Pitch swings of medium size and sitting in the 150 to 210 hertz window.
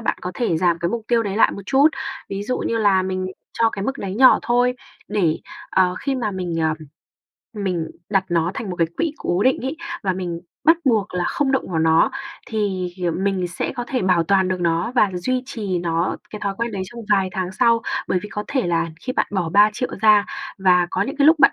Yes: average, 4.5 semitones; high, 195 Hz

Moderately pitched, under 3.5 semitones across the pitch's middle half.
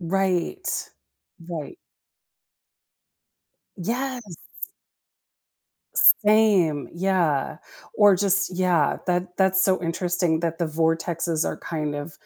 Yes: medium, 175 Hz; average, 2.9 semitones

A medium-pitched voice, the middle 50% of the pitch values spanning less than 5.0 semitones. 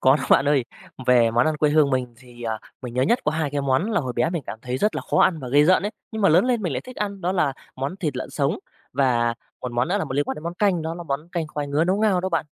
No: medium, 150 Hz; wide, 5.5 semitones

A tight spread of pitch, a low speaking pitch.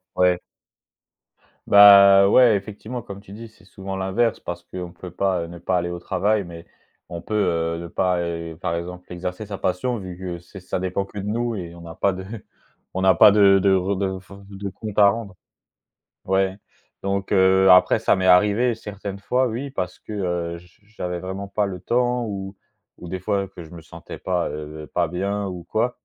Yes: narrow, 2.3 semitones; very low, 95 Hz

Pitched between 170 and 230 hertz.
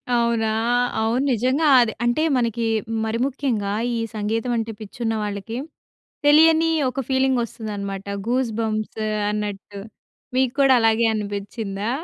Yes: high, 225 Hz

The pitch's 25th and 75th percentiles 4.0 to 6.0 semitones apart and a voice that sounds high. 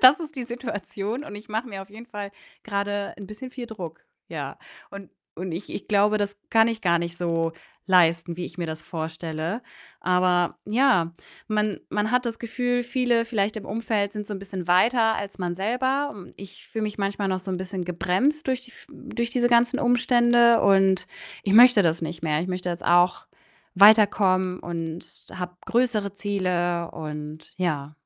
Yes: average, 4.6 semitones; high, 200 Hz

